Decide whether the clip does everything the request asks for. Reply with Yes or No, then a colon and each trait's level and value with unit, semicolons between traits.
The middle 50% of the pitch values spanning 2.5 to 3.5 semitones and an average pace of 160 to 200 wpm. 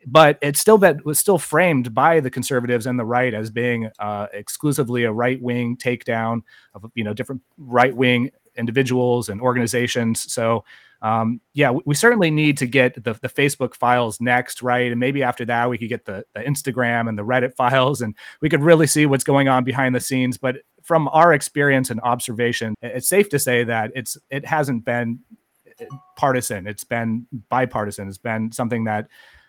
Yes: average, 2.8 semitones; average, 190 wpm